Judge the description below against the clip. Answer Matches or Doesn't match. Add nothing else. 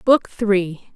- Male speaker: Doesn't match